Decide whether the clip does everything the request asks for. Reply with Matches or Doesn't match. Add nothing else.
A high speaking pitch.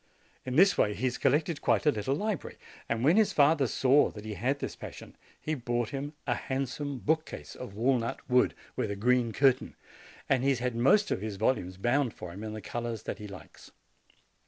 Doesn't match